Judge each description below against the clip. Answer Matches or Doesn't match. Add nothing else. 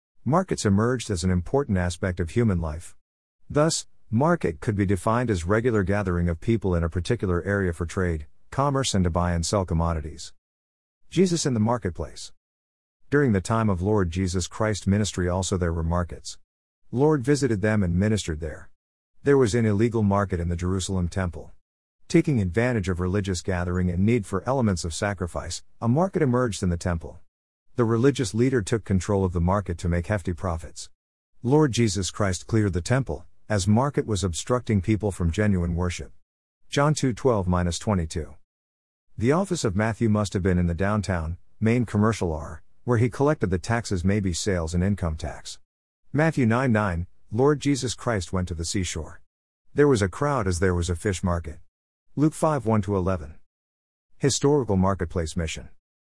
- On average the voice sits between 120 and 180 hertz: Doesn't match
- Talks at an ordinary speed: Matches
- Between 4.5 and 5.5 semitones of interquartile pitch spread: Matches